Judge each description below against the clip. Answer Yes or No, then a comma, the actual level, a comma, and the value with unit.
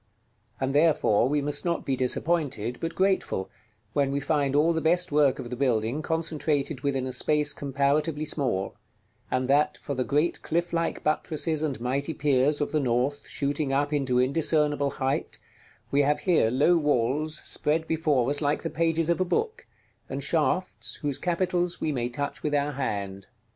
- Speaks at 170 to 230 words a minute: Yes, average, 175 wpm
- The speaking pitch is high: No, medium, 145 Hz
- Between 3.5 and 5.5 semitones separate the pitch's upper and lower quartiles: No, average, 3.0 semitones